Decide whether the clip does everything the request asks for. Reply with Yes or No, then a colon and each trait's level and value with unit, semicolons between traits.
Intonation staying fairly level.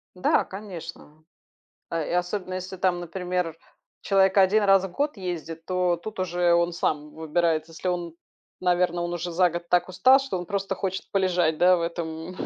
Yes: narrow, 1.9 semitones